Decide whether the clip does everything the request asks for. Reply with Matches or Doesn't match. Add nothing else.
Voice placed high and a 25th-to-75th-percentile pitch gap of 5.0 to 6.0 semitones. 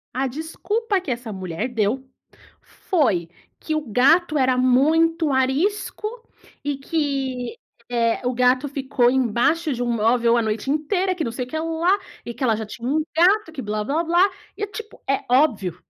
Matches